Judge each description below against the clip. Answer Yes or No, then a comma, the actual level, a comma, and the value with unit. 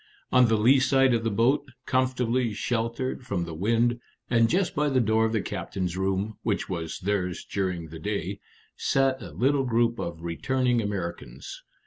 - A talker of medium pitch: No, low, 115 Hz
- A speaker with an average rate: Yes, average, 170 wpm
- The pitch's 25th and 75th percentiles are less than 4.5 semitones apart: No, average, 5.0 semitones